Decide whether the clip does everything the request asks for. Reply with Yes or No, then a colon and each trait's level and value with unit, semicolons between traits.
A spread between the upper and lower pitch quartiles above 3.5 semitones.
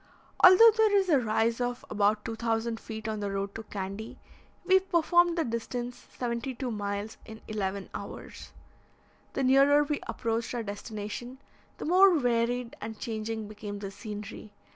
Yes: average, 4.0 semitones